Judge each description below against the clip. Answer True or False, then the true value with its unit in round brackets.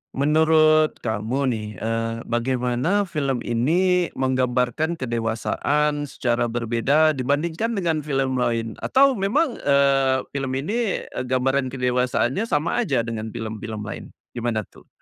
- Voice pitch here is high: False (130 Hz)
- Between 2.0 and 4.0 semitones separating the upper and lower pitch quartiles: False (4.7 semitones)